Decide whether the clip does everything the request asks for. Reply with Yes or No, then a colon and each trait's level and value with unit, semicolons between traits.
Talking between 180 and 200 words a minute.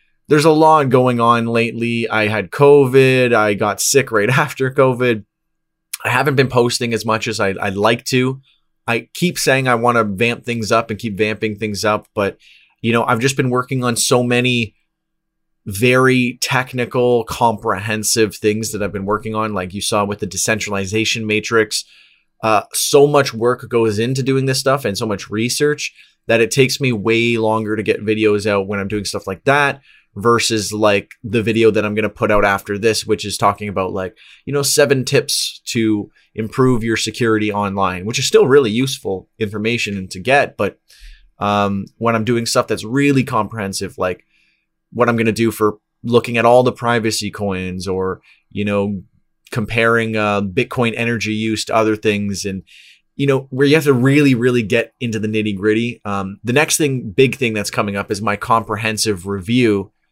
Yes: average, 190 wpm